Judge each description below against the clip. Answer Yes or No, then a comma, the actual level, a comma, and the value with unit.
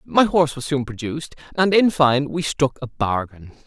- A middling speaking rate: Yes, average, 195 wpm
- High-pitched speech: No, medium, 140 Hz